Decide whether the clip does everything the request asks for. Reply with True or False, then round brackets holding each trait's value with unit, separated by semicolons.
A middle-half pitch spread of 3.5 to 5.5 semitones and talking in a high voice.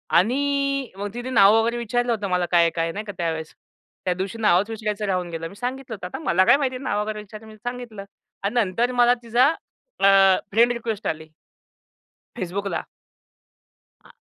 True (4.4 semitones; 215 Hz)